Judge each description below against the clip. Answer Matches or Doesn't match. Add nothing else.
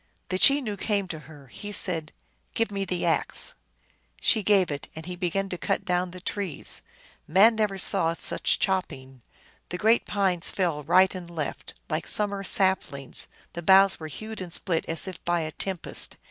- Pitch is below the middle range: Doesn't match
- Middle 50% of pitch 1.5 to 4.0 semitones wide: Matches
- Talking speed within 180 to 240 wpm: Matches